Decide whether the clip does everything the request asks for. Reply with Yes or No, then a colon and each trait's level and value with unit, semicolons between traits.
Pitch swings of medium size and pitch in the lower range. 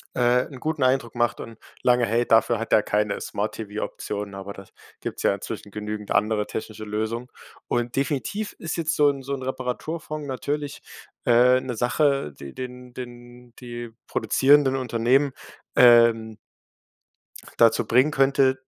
Yes: average, 3.1 semitones; low, 120 Hz